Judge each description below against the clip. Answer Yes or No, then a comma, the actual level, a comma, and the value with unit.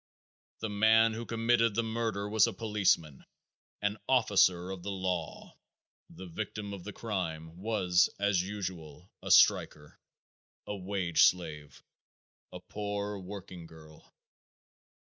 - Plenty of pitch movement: No, average, 3.2 semitones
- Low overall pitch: Yes, low, 100 Hz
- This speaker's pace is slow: Yes, slow, 120 wpm